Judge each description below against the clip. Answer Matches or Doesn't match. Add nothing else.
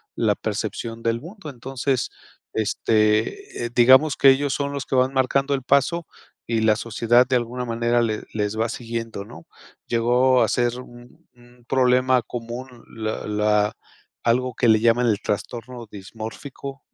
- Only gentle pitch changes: Matches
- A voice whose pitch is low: Matches